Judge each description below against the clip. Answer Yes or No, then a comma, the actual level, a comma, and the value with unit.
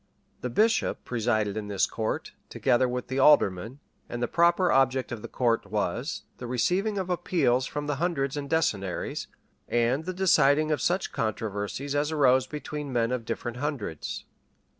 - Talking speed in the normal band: Yes, average, 160 wpm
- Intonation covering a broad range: No, average, 4.5 semitones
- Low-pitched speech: Yes, low, 130 Hz